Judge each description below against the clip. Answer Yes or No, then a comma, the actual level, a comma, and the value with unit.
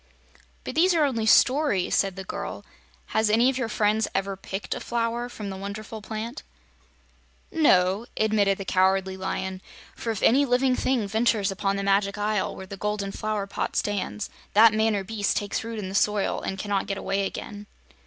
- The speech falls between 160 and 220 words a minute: Yes, average, 185 wpm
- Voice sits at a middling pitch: No, high, 210 Hz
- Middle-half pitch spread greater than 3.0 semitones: No, narrow, 2.4 semitones